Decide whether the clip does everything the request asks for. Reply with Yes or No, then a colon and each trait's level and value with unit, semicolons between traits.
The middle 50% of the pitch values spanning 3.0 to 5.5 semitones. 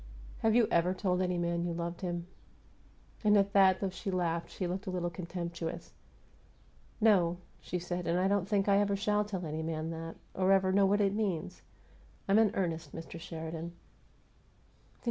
No: narrow, 2.6 semitones